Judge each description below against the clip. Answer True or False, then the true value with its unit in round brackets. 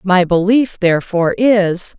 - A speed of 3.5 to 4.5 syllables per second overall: True (4.4 syllables/s)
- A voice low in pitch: False (195 Hz)